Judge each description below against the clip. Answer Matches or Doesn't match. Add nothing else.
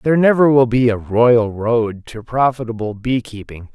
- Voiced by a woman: Doesn't match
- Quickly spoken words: Doesn't match